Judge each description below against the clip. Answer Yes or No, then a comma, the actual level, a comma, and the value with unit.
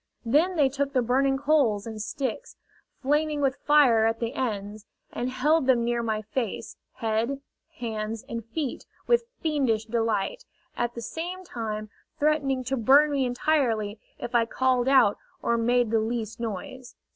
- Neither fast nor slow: Yes, average, 155 wpm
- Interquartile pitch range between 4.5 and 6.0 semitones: No, average, 3.7 semitones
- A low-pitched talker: No, high, 245 Hz